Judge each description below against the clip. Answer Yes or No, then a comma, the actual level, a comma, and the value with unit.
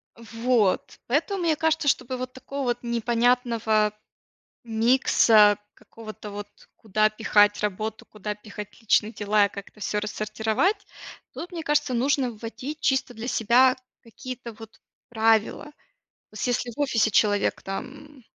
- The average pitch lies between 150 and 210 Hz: No, high, 230 Hz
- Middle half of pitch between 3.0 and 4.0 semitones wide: Yes, average, 3.3 semitones